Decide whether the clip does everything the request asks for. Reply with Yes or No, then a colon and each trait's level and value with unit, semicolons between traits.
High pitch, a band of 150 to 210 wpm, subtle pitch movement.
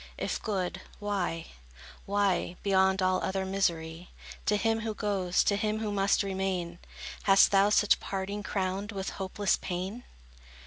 No: high, 195 Hz; average, 140 wpm; narrow, 1.7 semitones